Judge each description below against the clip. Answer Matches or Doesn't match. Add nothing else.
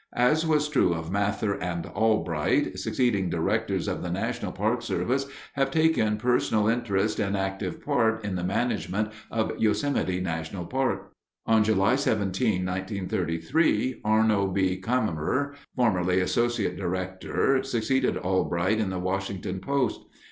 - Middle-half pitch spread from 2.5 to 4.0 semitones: Doesn't match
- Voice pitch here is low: Matches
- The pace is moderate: Doesn't match